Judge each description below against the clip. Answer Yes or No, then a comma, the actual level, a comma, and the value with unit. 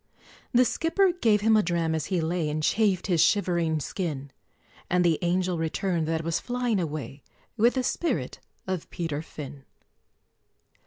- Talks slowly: No, average, 155 wpm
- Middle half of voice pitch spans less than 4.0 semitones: No, average, 5.0 semitones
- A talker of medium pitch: Yes, medium, 175 Hz